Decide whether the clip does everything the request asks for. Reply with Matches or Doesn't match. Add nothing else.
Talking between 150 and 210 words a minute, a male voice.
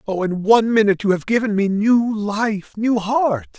Matches